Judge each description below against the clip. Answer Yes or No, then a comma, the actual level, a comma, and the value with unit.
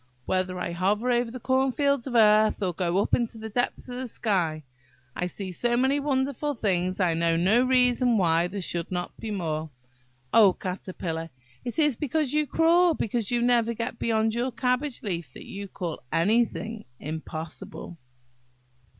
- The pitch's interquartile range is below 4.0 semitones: No, wide, 5.6 semitones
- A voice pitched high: Yes, high, 220 Hz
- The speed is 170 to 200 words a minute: Yes, average, 175 wpm